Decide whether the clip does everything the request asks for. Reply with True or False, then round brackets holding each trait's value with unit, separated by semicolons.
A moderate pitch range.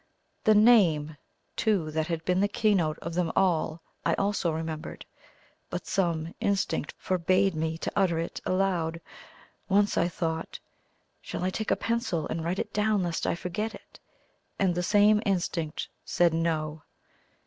True (3.5 semitones)